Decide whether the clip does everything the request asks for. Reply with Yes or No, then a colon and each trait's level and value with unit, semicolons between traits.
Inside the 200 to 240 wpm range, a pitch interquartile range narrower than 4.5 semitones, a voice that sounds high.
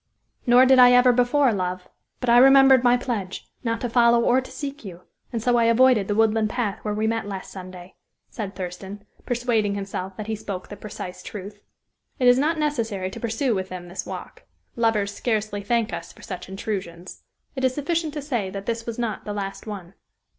Yes: fast, 205 wpm; average, 3.9 semitones; high, 225 Hz